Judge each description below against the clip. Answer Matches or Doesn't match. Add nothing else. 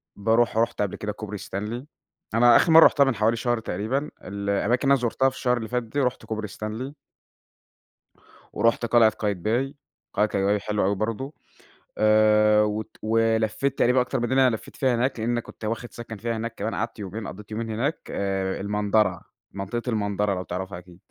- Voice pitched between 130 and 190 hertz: Doesn't match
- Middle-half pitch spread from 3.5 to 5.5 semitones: Doesn't match